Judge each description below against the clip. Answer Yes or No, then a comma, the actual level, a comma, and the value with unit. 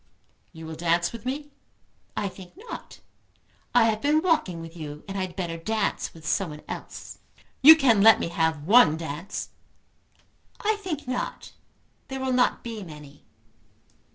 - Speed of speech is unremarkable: Yes, average, 155 wpm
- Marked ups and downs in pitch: Yes, wide, 7.8 semitones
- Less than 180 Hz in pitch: No, high, 195 Hz